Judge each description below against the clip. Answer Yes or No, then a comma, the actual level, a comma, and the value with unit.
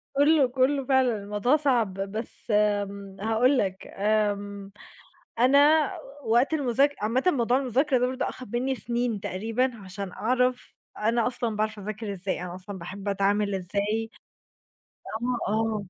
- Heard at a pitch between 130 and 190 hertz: No, high, 225 Hz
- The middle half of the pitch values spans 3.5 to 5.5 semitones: Yes, average, 4.0 semitones